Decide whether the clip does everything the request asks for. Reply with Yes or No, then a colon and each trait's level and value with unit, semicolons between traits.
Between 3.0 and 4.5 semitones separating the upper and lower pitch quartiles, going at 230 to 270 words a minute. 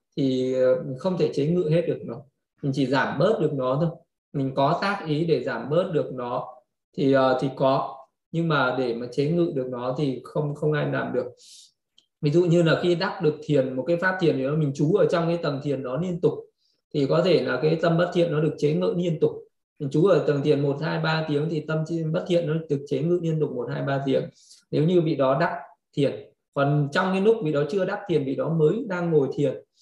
Yes: average, 3.5 semitones; fast, 250 wpm